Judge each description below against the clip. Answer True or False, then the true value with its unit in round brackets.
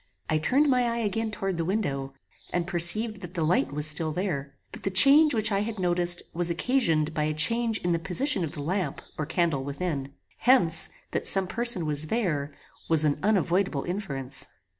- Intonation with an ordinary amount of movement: False (5.7 semitones)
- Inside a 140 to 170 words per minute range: False (190 wpm)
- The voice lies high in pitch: False (175 Hz)